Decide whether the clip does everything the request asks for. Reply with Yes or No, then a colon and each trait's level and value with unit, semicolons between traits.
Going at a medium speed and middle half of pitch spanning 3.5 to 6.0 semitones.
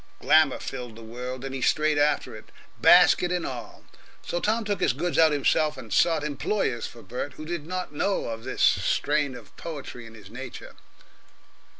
Yes: average, 185 wpm; average, 5.1 semitones